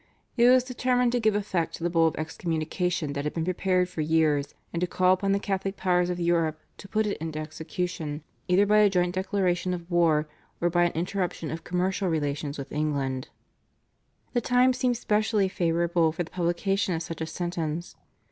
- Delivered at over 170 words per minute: Yes, average, 195 wpm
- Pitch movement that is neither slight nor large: Yes, average, 3.3 semitones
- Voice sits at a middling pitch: Yes, medium, 175 Hz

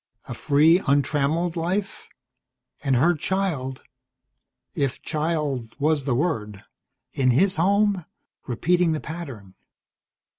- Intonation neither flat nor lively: Yes, average, 4.7 semitones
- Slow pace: Yes, slow, 105 wpm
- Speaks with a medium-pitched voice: Yes, medium, 155 Hz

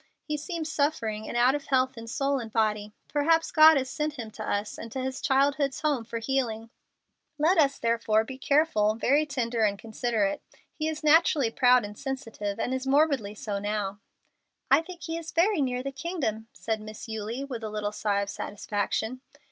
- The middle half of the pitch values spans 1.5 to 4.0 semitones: No, average, 4.9 semitones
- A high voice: Yes, very high, 255 Hz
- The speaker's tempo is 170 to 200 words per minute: Yes, average, 190 wpm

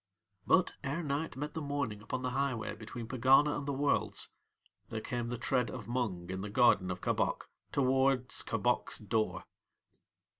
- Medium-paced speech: Yes, average, 160 wpm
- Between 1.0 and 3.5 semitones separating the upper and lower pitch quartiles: No, average, 3.9 semitones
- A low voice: Yes, low, 125 Hz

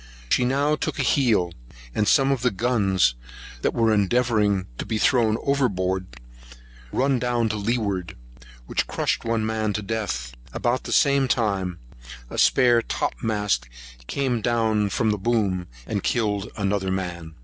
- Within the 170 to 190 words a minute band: No, average, 150 wpm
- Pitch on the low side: Yes, low, 110 Hz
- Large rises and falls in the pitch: No, average, 3.8 semitones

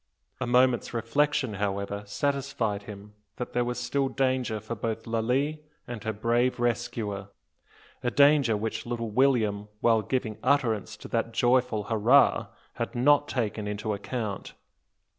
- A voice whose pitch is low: Yes, low, 115 Hz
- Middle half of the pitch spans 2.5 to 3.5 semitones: Yes, average, 3.2 semitones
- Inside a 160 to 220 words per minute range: No, average, 140 wpm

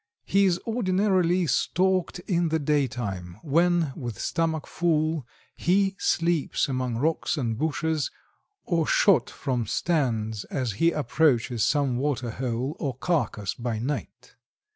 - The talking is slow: Yes, slow, 125 wpm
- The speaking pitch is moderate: Yes, medium, 150 Hz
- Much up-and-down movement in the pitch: Yes, wide, 5.7 semitones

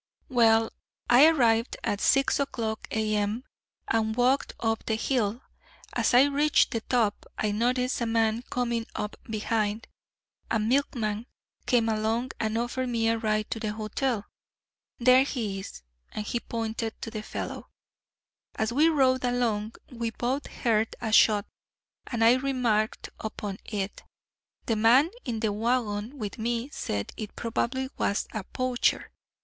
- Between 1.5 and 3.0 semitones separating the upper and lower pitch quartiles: Yes, narrow, 2.5 semitones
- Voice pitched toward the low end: No, high, 230 Hz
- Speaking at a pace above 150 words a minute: No, average, 145 wpm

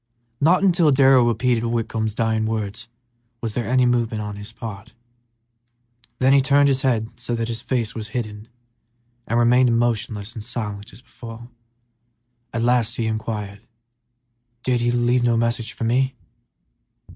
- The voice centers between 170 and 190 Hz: No, low, 115 Hz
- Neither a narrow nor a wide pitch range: No, narrow, 2.2 semitones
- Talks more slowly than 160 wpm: Yes, average, 150 wpm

